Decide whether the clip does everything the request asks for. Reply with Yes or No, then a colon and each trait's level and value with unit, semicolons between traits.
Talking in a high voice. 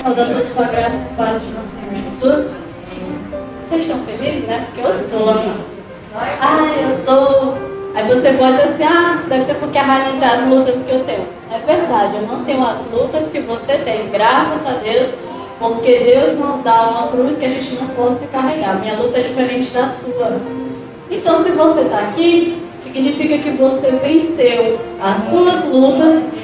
Yes: very high, 260 Hz